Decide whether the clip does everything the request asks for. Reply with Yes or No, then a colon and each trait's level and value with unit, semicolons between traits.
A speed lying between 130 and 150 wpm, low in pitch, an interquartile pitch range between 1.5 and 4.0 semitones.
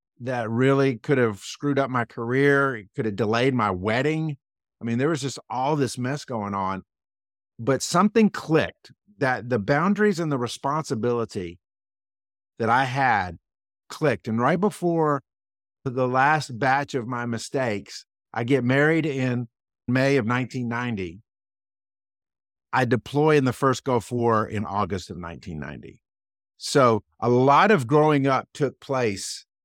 No: average, 145 wpm; low, 125 Hz; average, 5.0 semitones